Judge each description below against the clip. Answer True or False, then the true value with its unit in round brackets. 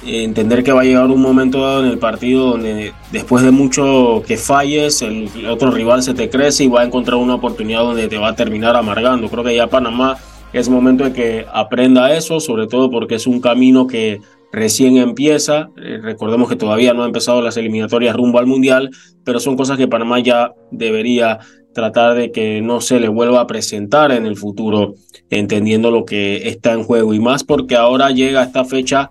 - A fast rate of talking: True (200 wpm)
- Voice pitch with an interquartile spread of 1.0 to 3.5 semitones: True (2.5 semitones)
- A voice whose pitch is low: True (120 Hz)